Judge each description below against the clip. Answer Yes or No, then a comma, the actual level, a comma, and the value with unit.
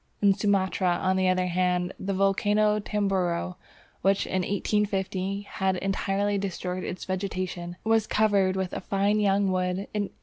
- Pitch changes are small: Yes, narrow, 1.6 semitones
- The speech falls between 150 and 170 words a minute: Yes, average, 160 wpm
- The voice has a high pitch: Yes, high, 195 Hz